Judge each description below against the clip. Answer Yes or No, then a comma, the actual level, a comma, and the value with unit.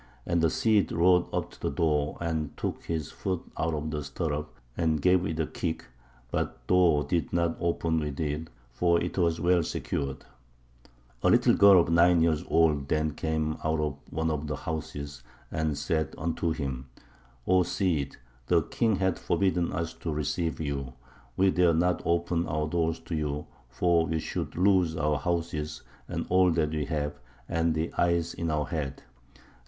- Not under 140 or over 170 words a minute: No, average, 180 wpm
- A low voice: Yes, very low, 80 Hz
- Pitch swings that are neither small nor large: No, narrow, 2.1 semitones